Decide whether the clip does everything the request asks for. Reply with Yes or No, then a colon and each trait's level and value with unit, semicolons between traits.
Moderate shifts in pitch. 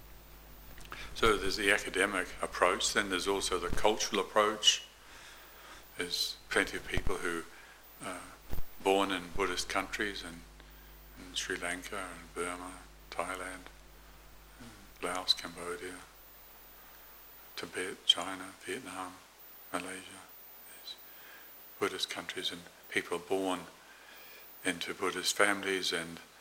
No: narrow, 2.2 semitones